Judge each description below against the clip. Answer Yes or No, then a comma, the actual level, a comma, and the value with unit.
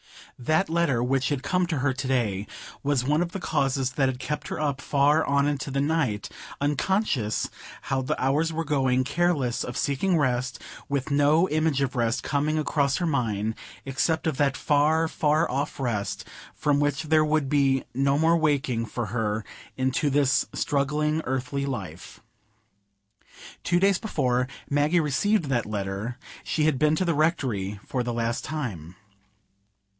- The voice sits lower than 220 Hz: Yes, medium, 140 Hz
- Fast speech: No, average, 165 wpm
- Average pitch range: Yes, average, 3.5 semitones